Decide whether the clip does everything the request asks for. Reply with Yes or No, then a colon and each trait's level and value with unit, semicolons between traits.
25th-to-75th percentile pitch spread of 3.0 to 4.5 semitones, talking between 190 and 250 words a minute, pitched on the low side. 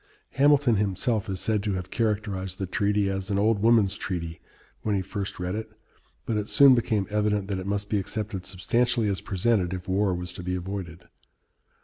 No: narrow, 2.6 semitones; average, 195 wpm; low, 100 Hz